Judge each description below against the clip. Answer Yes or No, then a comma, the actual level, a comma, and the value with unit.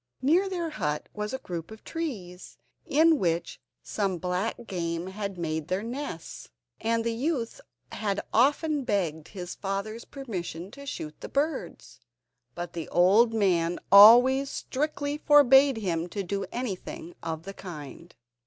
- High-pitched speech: Yes, high, 205 Hz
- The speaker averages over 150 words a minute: No, average, 145 wpm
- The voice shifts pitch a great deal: Yes, wide, 7.2 semitones